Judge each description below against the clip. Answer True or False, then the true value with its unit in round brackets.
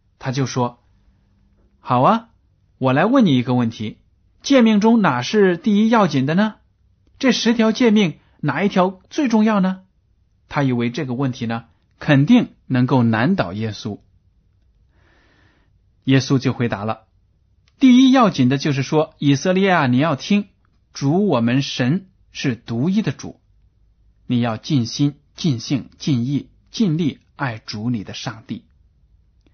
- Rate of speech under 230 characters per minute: True (200 characters per minute)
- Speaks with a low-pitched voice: True (130 Hz)